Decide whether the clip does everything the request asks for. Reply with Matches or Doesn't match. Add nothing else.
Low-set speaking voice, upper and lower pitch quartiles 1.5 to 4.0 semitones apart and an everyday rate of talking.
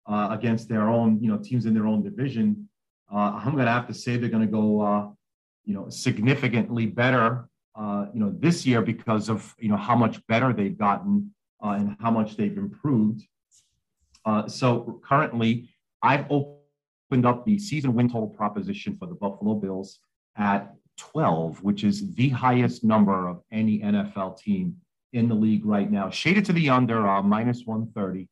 Matches